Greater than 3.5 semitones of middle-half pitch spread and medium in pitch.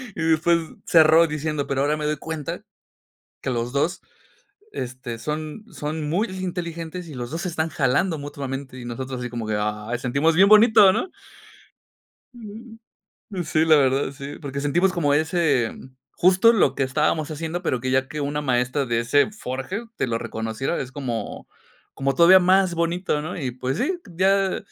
Yes: average, 4.8 semitones; medium, 150 Hz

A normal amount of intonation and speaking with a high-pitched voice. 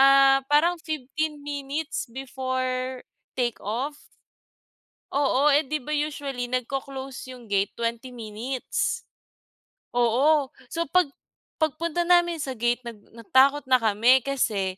Yes: average, 3.2 semitones; very high, 265 Hz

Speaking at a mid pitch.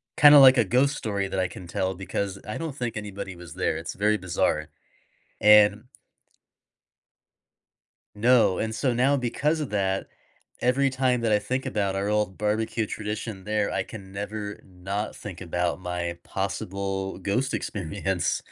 No: low, 105 Hz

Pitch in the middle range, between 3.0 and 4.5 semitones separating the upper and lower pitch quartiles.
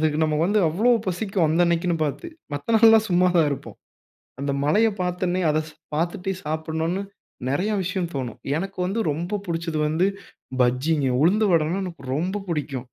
Yes: medium, 170 Hz; average, 3.5 semitones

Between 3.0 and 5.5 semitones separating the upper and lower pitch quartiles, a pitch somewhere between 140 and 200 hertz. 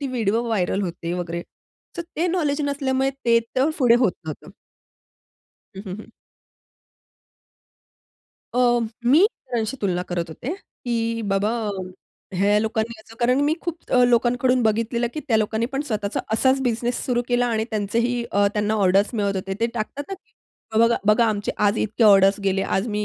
No: average, 3.5 semitones; high, 225 Hz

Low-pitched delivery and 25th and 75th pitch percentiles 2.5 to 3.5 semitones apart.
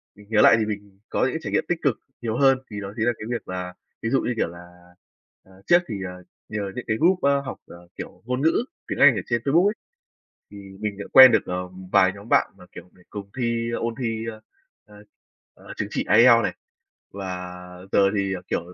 No: low, 110 Hz; average, 4.2 semitones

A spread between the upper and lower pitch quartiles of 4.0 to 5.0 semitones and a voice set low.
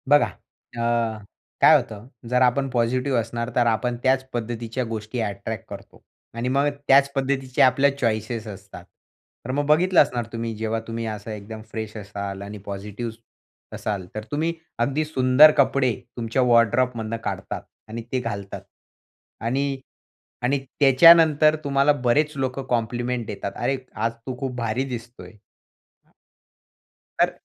No: average, 3.3 semitones; low, 120 Hz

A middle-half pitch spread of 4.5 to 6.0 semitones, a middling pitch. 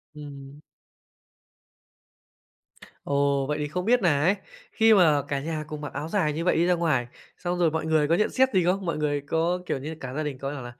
No: average, 3.5 semitones; medium, 155 Hz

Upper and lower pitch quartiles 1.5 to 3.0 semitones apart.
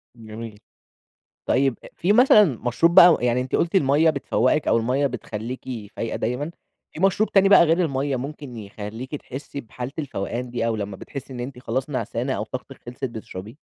No: average, 4.1 semitones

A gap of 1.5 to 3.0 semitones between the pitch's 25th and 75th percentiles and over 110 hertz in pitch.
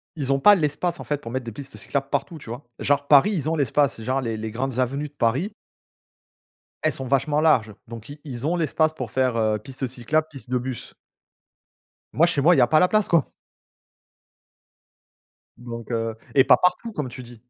No: average, 4.1 semitones; low, 135 Hz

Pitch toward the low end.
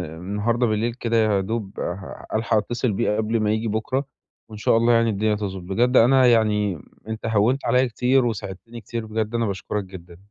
Yes: low, 110 Hz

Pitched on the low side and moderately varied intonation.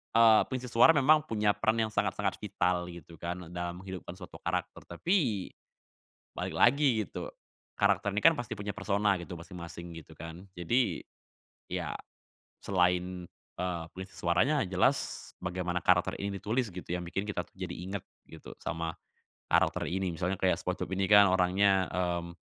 Yes: very low, 95 Hz; average, 3.1 semitones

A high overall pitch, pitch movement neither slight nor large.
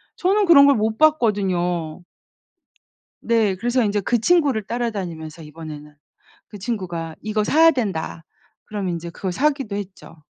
No: high, 205 Hz; wide, 6.0 semitones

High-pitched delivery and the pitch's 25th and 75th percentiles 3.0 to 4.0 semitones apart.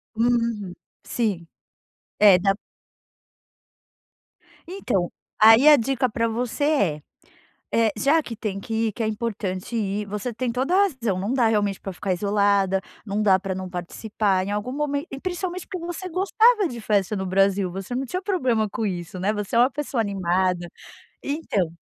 No: high, 215 Hz; average, 4.7 semitones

